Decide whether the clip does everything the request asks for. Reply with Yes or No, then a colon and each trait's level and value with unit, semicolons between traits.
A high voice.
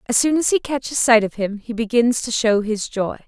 Yes: high, 230 Hz